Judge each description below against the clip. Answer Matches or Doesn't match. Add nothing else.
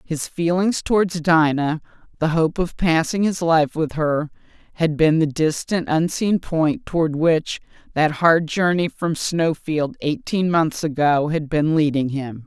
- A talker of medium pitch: Matches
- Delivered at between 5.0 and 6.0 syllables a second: Doesn't match